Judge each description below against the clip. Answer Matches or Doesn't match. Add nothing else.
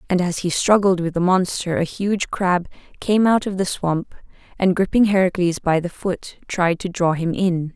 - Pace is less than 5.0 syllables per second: Matches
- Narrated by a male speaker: Doesn't match